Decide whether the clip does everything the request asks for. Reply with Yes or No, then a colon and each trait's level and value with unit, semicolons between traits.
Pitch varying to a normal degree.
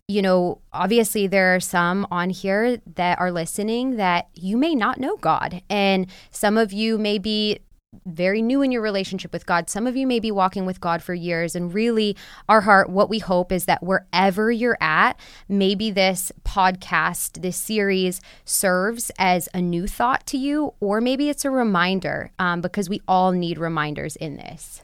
Yes: average, 3.3 semitones